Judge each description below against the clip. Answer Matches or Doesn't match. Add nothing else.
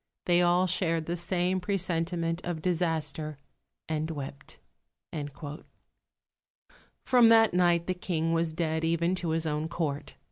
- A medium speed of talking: Doesn't match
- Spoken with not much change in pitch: Matches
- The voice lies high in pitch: Doesn't match